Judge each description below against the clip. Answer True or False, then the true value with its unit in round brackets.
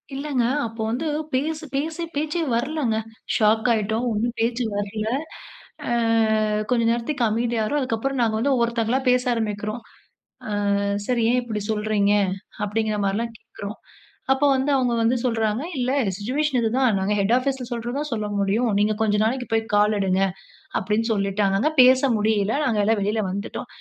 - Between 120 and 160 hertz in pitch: False (230 Hz)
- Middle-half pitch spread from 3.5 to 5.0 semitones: False (3.1 semitones)